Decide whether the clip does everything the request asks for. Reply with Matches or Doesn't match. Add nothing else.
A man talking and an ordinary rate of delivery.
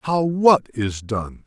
Matches